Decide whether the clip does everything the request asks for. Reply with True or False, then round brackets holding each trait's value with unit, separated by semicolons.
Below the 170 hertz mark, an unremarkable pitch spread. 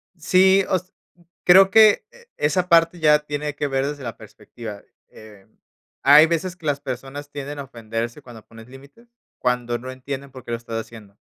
False (140 Hz; 5.7 semitones)